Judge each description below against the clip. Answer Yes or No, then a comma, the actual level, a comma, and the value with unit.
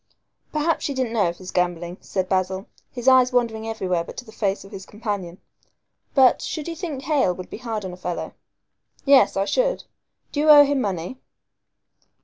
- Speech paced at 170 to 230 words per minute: Yes, average, 190 wpm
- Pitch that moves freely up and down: Yes, wide, 6.3 semitones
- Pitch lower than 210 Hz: No, high, 220 Hz